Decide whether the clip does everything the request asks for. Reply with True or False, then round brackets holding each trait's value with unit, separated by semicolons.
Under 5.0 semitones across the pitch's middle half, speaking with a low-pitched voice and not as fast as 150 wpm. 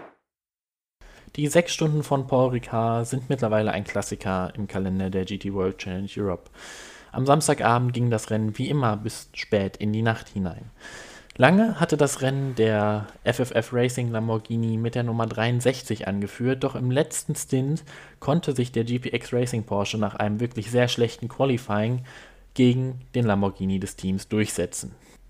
False (3.8 semitones; 115 Hz; 155 wpm)